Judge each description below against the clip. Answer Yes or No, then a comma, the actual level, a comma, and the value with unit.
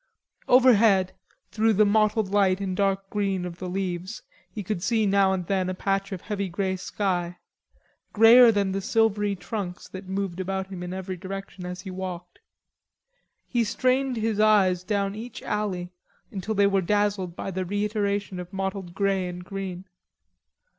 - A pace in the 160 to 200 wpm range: Yes, average, 165 wpm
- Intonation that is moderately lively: No, narrow, 2.0 semitones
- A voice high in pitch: Yes, high, 195 Hz